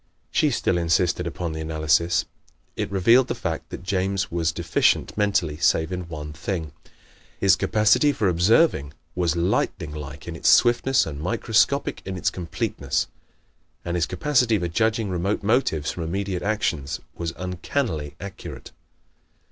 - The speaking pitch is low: Yes, very low, 90 Hz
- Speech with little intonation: No, average, 4.3 semitones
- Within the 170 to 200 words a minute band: No, average, 145 wpm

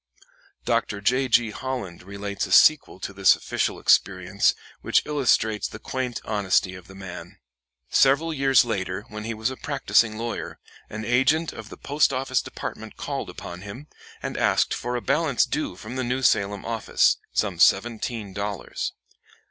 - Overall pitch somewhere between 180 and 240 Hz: No, low, 110 Hz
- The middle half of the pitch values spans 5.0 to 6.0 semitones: No, average, 4.6 semitones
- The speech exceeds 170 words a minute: No, average, 160 wpm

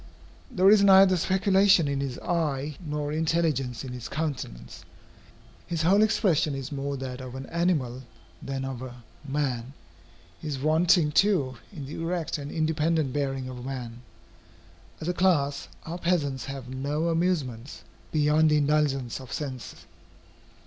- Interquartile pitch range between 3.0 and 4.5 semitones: Yes, average, 4.0 semitones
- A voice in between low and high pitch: Yes, medium, 145 Hz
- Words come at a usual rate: Yes, average, 150 wpm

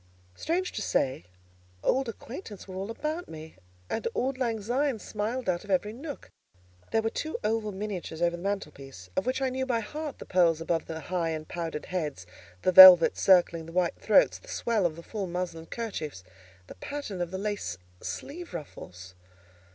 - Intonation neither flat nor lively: No, wide, 6.0 semitones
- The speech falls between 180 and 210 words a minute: Yes, average, 185 wpm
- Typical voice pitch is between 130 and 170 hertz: No, high, 190 Hz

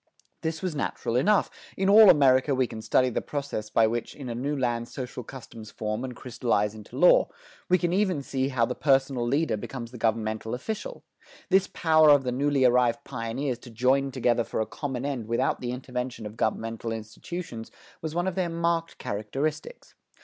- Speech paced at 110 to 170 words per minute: No, average, 190 wpm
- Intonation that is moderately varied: Yes, average, 4.3 semitones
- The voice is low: Yes, low, 130 Hz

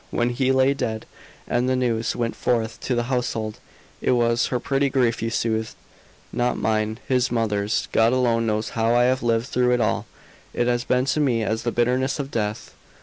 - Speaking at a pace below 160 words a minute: No, average, 200 wpm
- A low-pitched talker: Yes, low, 120 Hz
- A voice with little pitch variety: Yes, narrow, 2.0 semitones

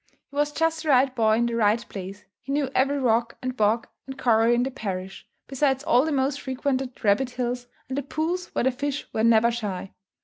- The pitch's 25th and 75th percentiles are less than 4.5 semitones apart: Yes, average, 3.4 semitones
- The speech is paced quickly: Yes, fast, 215 wpm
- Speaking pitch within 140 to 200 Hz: No, very high, 255 Hz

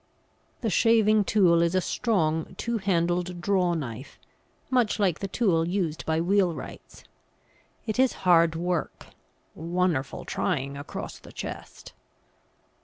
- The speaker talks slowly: Yes, slow, 120 wpm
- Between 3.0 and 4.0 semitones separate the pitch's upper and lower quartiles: Yes, average, 3.6 semitones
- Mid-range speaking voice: Yes, medium, 175 Hz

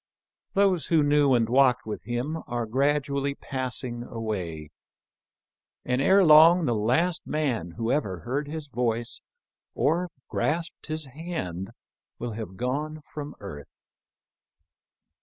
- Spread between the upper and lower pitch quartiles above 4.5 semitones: Yes, average, 5.1 semitones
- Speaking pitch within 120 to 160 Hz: Yes, low, 135 Hz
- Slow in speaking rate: Yes, slow, 120 wpm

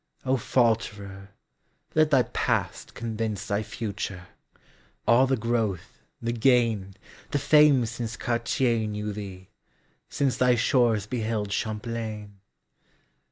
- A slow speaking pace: Yes, slow, 95 wpm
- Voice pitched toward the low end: Yes, low, 115 Hz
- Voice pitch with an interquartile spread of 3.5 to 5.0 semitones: No, average, 2.8 semitones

